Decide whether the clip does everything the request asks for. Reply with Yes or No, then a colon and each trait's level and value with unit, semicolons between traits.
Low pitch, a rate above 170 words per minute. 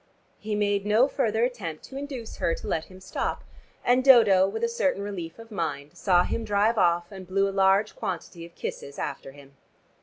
No: high, 200 Hz; average, 195 wpm